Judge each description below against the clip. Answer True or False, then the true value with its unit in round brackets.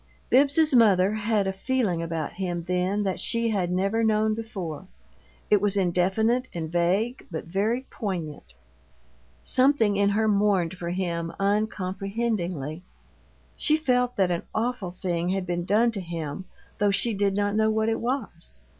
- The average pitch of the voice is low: False (200 Hz)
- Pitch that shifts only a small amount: False (3.8 semitones)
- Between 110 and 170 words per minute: True (155 wpm)